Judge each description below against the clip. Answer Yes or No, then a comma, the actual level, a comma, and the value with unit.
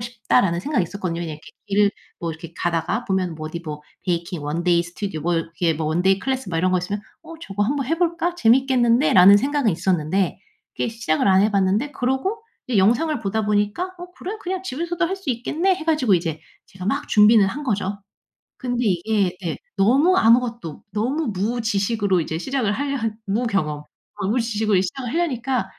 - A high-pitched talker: Yes, high, 210 Hz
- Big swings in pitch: Yes, wide, 6.6 semitones